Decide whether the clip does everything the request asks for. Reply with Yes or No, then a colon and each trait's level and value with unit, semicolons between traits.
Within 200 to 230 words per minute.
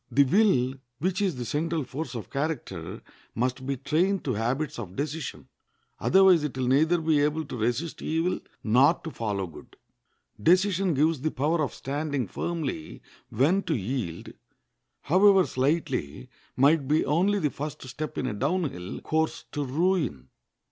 No: average, 155 wpm